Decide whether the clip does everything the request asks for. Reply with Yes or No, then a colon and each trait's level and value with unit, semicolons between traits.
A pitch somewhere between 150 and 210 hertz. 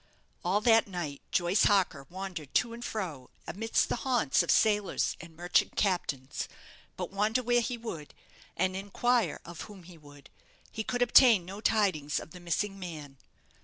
Yes: high, 190 Hz